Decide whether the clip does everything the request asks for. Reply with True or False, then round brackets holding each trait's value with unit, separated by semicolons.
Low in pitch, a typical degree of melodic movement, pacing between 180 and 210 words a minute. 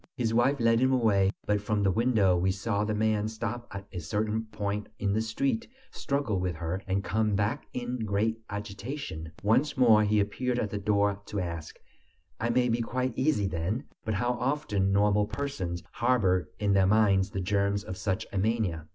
True (105 Hz; 3.1 semitones; 190 wpm)